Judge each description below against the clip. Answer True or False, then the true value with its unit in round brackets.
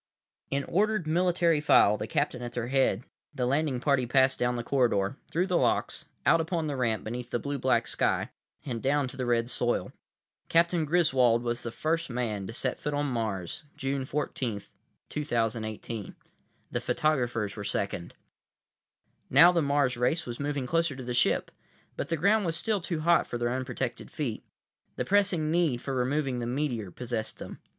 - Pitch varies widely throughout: False (4.5 semitones)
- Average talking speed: True (180 wpm)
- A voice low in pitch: True (130 Hz)